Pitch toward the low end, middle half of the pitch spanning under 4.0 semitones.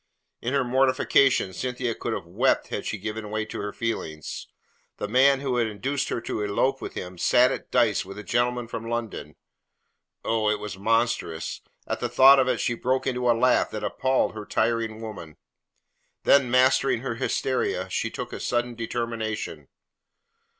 Yes: low, 115 Hz; average, 3.0 semitones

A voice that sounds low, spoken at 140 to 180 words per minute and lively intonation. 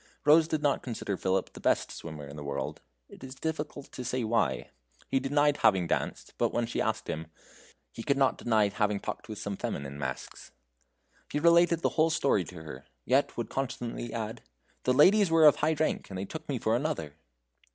No: low, 120 Hz; average, 200 wpm; wide, 7.5 semitones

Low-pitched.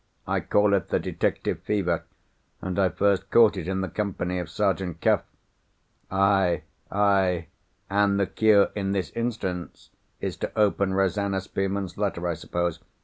Yes: very low, 95 Hz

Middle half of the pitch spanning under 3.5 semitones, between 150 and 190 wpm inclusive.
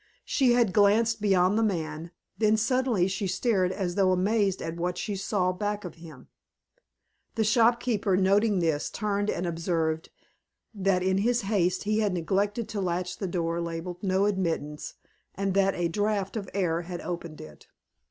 Yes: average, 3.1 semitones; average, 165 wpm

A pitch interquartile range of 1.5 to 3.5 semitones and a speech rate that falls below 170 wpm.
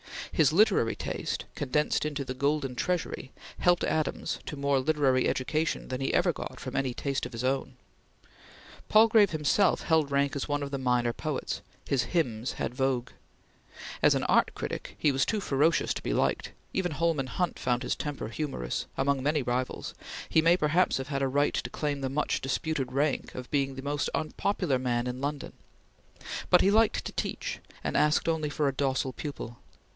No: average, 3.0 semitones; average, 185 wpm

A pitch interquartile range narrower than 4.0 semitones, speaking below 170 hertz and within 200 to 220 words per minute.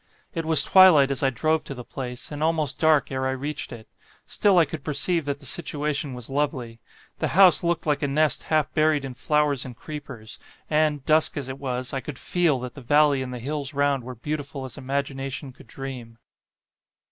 Yes: narrow, 2.6 semitones; medium, 140 Hz; fast, 205 wpm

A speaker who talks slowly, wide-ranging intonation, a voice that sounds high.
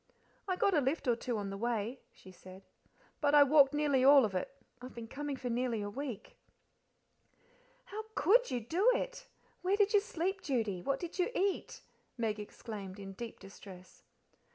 No: average, 180 wpm; wide, 7.5 semitones; very high, 255 Hz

